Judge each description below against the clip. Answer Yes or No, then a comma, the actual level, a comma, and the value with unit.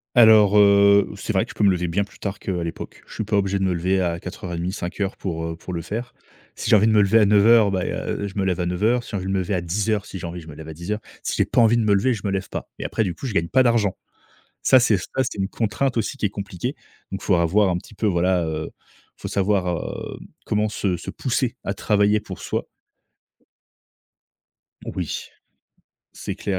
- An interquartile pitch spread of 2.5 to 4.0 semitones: Yes, average, 3.1 semitones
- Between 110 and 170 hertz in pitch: No, low, 100 Hz